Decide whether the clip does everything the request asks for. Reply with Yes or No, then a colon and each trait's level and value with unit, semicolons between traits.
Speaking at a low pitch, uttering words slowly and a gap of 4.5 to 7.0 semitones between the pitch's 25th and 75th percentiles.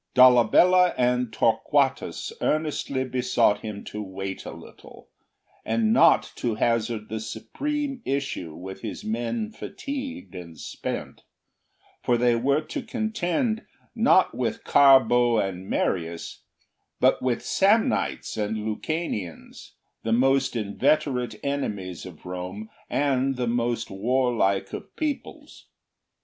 Yes: low, 120 Hz; slow, 115 wpm; average, 5.1 semitones